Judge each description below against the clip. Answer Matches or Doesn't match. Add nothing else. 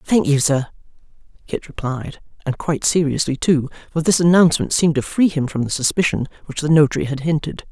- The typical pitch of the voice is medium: Matches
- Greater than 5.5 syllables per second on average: Matches